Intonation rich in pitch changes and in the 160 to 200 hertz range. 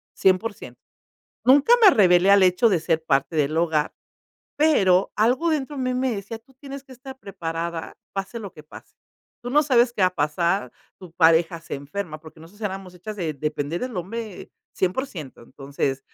Yes: wide, 6.5 semitones; medium, 185 Hz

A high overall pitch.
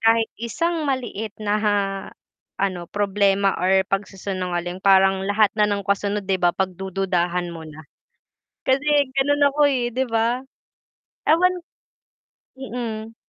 Yes: high, 205 Hz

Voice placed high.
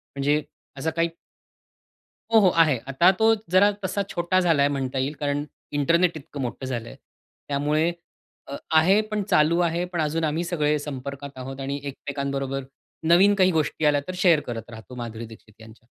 No: medium, 150 Hz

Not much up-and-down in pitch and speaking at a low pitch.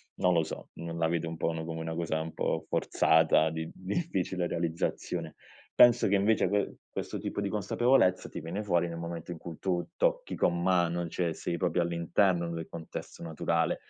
Yes: narrow, 2.3 semitones; very low, 85 Hz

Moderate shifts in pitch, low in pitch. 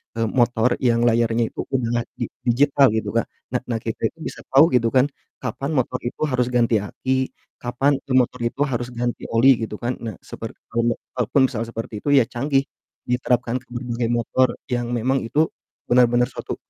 No: narrow, 1.6 semitones; low, 120 Hz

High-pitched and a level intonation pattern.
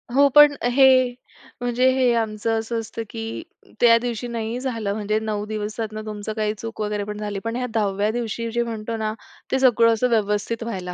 Yes: high, 225 Hz; narrow, 1.9 semitones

